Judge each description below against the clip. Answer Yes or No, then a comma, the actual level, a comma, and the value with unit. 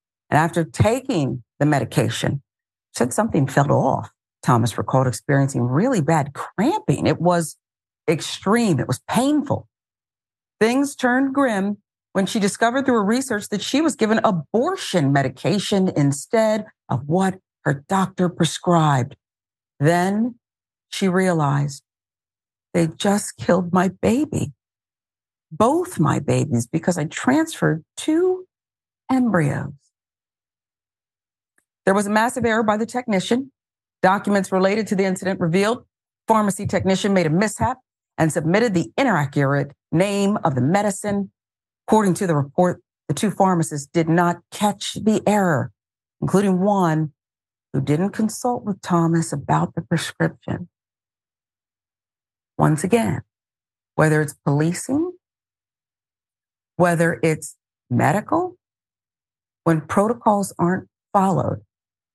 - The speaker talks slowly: Yes, slow, 115 wpm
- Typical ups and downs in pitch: No, wide, 7.3 semitones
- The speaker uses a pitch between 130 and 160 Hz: No, medium, 170 Hz